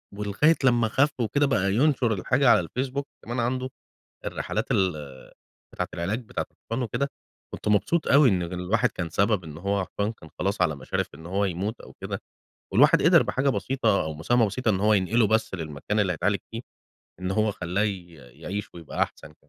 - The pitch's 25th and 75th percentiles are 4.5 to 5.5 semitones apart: Yes, average, 4.9 semitones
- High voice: No, low, 105 Hz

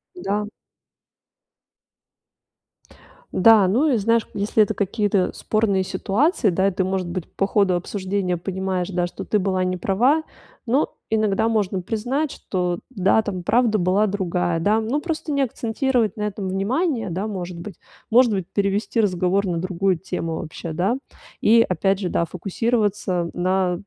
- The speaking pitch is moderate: No, high, 195 Hz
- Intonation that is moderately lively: Yes, average, 3.3 semitones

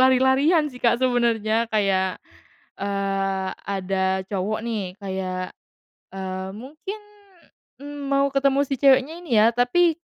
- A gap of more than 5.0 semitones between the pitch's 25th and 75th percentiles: Yes, wide, 5.4 semitones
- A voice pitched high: Yes, high, 225 Hz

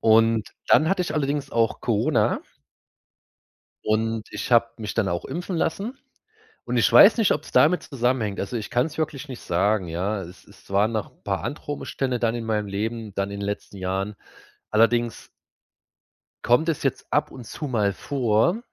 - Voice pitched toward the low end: Yes, low, 115 Hz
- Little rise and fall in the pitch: No, average, 5.3 semitones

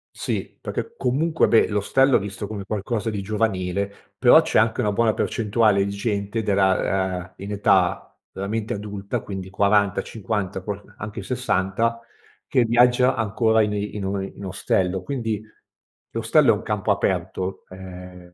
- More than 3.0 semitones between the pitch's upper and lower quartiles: No, narrow, 2.6 semitones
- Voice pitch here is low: Yes, low, 100 Hz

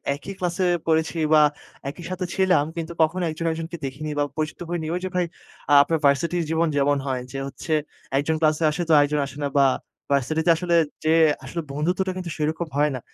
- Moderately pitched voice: Yes, medium, 160 Hz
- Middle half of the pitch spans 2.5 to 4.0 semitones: Yes, average, 2.8 semitones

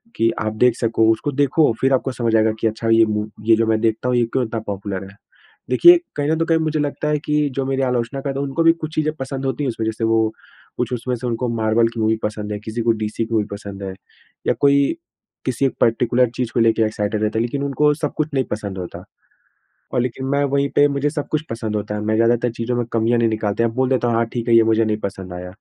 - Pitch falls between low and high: No, low, 115 Hz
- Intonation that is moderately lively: Yes, average, 3.6 semitones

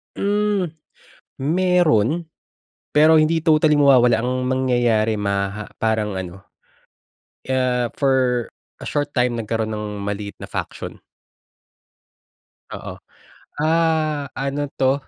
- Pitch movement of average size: No, wide, 5.7 semitones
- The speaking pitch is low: Yes, low, 130 Hz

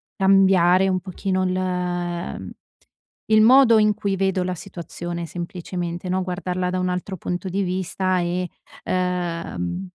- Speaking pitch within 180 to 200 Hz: Yes, medium, 185 Hz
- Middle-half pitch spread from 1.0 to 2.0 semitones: Yes, narrow, 1.4 semitones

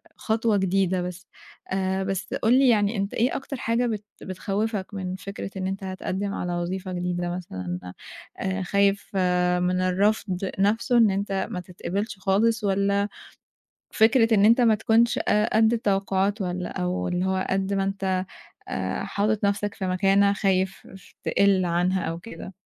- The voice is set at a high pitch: Yes, high, 195 Hz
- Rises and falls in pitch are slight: Yes, narrow, 2.0 semitones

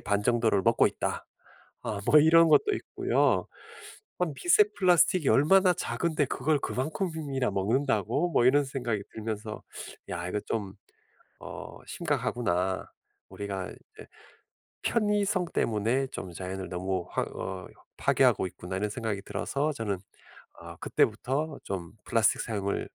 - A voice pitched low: Yes, low, 120 Hz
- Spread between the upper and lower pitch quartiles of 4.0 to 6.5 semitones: No, wide, 7.4 semitones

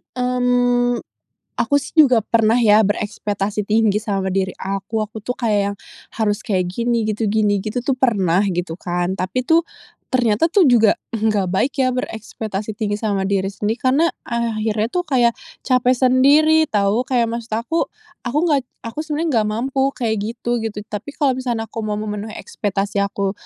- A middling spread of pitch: Yes, average, 3.4 semitones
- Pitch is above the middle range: Yes, high, 225 Hz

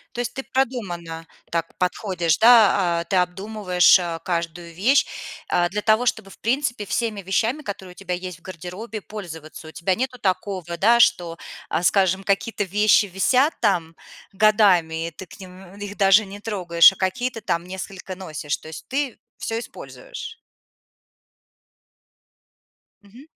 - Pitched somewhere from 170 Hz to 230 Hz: Yes, high, 190 Hz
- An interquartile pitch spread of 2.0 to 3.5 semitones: No, average, 3.9 semitones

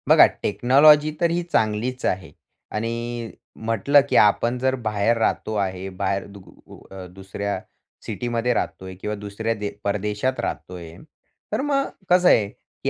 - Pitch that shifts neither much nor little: Yes, average, 3.9 semitones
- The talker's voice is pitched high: No, low, 110 Hz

